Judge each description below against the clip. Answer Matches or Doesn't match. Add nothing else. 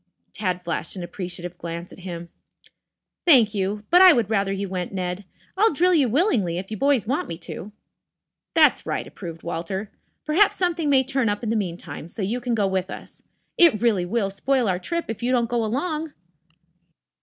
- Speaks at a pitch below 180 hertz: Doesn't match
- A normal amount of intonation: Doesn't match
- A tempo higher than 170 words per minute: Matches